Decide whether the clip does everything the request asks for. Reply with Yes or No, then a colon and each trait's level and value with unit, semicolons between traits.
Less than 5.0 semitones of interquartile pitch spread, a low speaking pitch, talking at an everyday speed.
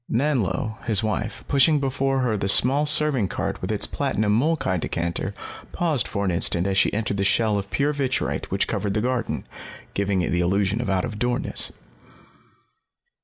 No: wide, 5.4 semitones; low, 110 Hz; average, 175 wpm